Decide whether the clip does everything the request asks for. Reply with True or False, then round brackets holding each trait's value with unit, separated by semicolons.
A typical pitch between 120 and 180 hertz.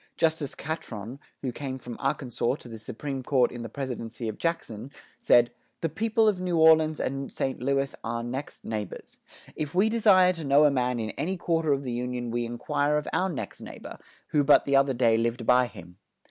True (135 Hz)